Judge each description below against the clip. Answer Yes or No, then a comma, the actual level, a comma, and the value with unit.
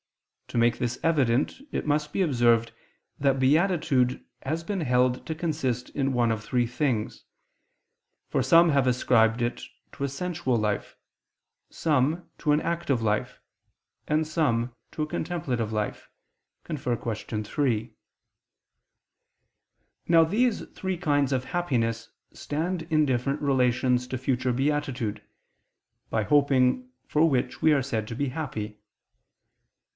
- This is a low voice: Yes, low, 130 Hz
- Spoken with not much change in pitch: No, average, 4.3 semitones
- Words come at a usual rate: No, slow, 130 wpm